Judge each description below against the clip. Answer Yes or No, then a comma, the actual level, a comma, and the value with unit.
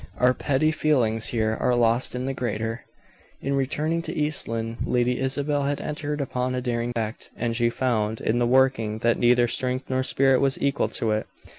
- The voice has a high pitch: No, low, 125 Hz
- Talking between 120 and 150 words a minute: No, average, 190 wpm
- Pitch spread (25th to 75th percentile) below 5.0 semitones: Yes, average, 2.8 semitones